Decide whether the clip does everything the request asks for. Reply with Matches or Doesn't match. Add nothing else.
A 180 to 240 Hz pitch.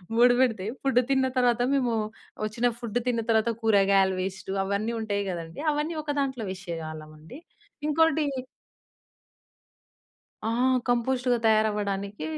Matches